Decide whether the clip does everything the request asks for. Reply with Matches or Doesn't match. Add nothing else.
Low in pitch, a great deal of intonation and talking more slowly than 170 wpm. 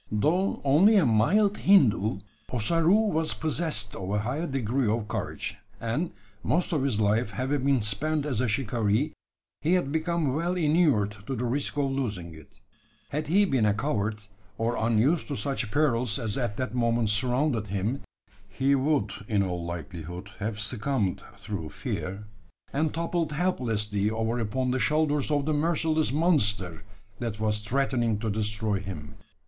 Matches